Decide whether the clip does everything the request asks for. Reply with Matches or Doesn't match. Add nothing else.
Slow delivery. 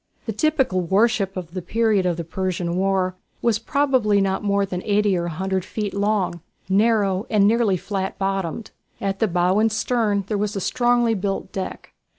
Doesn't match